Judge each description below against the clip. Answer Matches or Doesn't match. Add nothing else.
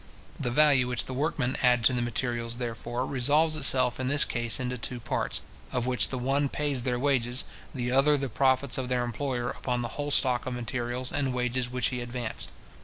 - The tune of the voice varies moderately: Doesn't match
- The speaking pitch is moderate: Doesn't match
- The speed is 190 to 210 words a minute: Matches